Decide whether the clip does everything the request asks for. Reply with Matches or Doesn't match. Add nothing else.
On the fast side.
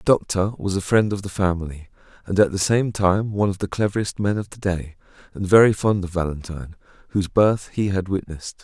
Matches